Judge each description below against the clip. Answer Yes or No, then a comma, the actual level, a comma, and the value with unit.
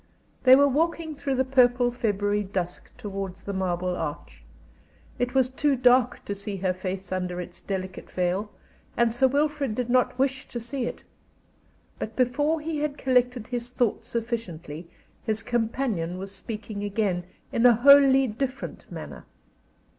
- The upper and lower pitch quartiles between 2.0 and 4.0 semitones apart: No, average, 5.1 semitones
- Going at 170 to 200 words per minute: No, average, 155 wpm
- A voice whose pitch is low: No, high, 235 Hz